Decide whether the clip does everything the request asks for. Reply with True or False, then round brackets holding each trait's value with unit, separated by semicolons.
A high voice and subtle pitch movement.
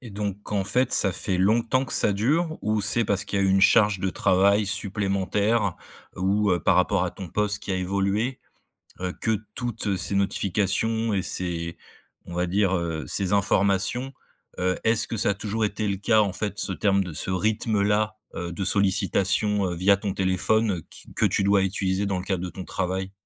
False (100 Hz; 2.1 semitones)